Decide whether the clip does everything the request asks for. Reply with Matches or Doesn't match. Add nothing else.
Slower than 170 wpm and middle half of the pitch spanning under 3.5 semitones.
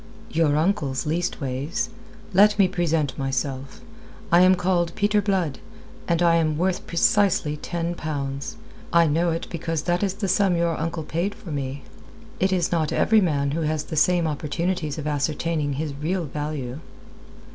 Matches